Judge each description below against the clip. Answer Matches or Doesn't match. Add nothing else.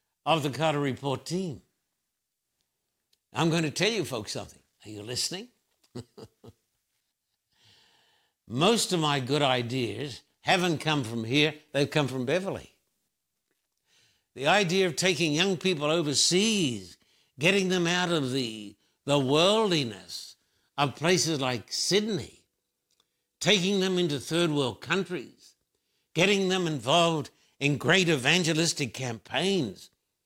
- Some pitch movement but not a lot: Doesn't match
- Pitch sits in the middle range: Matches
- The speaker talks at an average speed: Doesn't match